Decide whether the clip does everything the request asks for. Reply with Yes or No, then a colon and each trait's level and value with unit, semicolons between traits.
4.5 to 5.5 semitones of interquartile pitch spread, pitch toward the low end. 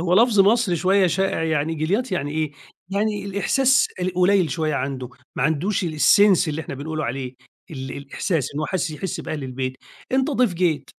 No: average, 5.2 semitones; medium, 170 Hz